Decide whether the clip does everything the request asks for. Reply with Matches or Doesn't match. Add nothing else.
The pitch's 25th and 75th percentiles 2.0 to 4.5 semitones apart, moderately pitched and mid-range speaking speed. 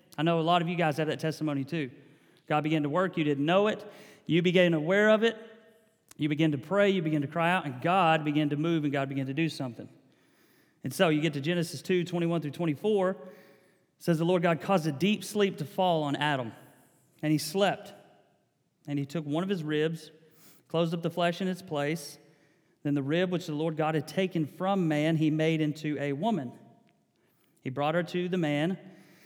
Doesn't match